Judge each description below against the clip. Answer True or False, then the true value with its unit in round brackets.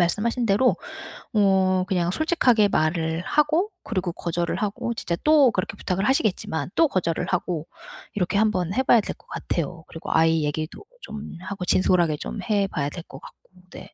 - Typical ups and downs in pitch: True (4.2 semitones)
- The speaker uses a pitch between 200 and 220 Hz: False (185 Hz)